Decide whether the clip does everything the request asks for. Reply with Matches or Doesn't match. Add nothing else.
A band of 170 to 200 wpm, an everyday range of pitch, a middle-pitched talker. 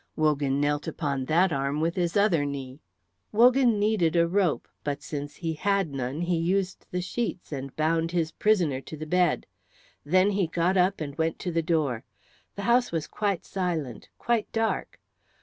Matches